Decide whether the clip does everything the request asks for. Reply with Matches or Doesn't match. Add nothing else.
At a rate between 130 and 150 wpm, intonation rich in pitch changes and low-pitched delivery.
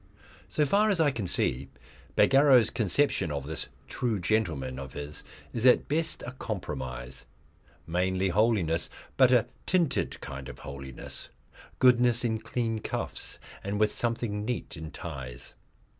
Matches